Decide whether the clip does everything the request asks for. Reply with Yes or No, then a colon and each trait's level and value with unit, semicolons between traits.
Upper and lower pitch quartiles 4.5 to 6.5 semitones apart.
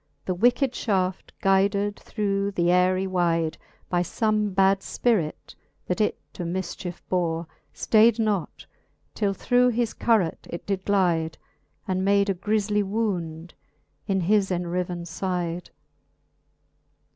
No: average, 2.9 semitones